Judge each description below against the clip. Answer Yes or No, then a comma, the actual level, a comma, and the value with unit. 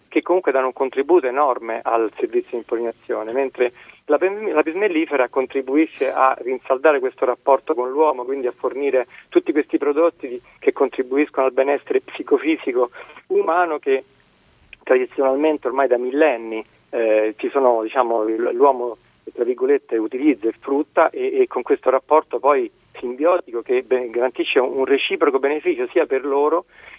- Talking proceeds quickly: No, average, 140 wpm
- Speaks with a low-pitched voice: No, medium, 155 Hz